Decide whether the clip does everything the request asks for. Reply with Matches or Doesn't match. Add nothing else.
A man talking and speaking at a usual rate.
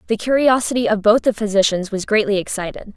Doesn't match